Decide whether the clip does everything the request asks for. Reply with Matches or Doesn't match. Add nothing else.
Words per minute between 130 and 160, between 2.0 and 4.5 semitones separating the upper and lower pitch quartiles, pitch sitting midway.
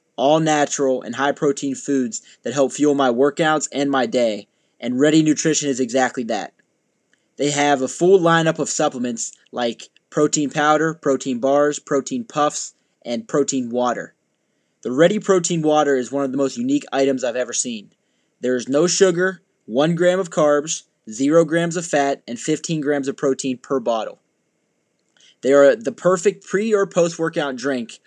Doesn't match